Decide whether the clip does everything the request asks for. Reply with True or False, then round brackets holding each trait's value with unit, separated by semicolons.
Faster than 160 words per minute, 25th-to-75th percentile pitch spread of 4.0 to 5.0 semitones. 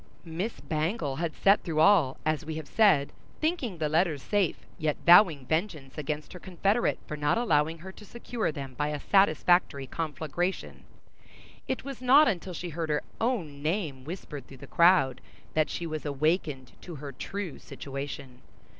True (170 wpm; 4.4 semitones)